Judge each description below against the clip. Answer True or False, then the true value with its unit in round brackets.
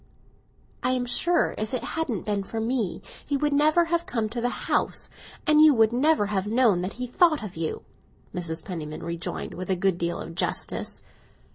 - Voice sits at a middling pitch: False (225 Hz)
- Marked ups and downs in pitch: True (7.4 semitones)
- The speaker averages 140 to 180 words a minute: False (190 wpm)